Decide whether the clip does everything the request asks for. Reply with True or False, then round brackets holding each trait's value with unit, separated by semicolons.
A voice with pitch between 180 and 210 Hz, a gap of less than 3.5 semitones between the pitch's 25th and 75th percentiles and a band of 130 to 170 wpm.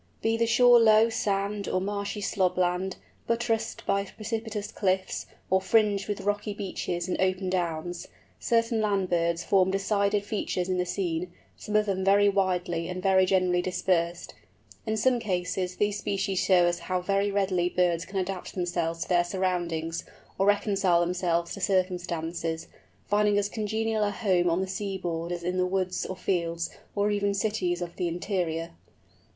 True (190 Hz; 2.5 semitones; 165 wpm)